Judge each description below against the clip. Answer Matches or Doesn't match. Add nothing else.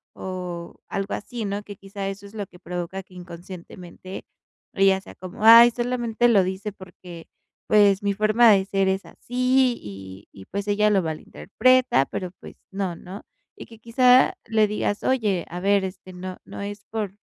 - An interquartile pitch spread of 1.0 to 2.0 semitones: Doesn't match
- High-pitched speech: Matches